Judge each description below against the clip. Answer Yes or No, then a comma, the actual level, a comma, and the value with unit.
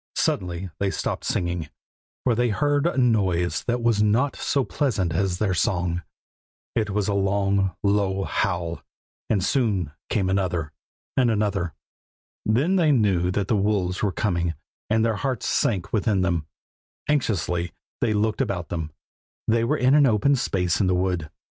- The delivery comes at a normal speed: Yes, average, 160 wpm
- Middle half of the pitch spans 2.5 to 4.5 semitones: Yes, average, 4.2 semitones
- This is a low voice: Yes, low, 100 Hz